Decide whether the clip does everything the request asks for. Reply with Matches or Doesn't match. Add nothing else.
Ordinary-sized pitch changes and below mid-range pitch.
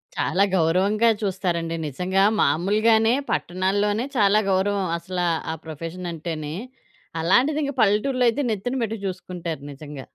Doesn't match